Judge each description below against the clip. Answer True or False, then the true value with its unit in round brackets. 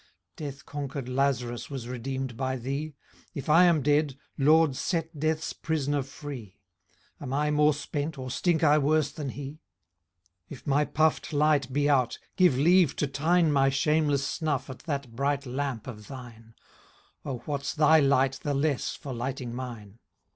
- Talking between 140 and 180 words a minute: True (160 wpm)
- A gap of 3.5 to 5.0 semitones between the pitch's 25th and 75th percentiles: False (2.5 semitones)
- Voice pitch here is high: False (140 Hz)